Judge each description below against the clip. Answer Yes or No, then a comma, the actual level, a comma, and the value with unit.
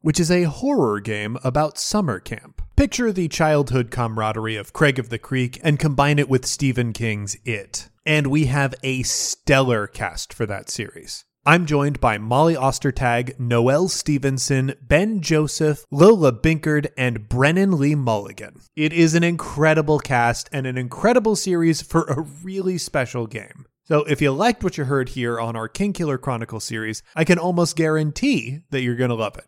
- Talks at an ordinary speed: Yes, average, 175 wpm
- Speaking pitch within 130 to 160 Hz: Yes, medium, 140 Hz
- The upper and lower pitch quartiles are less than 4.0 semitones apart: No, average, 4.8 semitones